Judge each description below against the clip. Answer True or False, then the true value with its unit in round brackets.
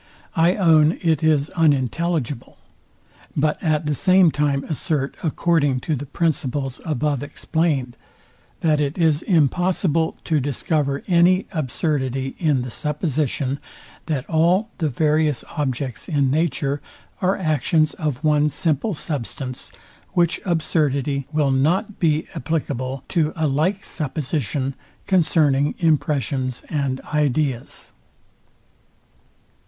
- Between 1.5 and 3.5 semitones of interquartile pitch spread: True (2.9 semitones)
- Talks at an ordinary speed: False (110 wpm)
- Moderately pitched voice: True (150 Hz)